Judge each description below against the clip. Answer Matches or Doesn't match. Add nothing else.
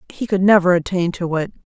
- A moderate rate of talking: Doesn't match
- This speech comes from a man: Doesn't match